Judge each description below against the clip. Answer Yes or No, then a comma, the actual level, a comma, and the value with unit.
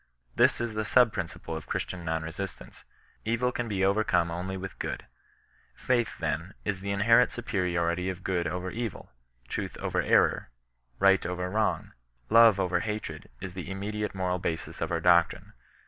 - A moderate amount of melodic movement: Yes, average, 3.4 semitones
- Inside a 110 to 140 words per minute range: No, average, 165 wpm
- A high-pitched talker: No, very low, 95 Hz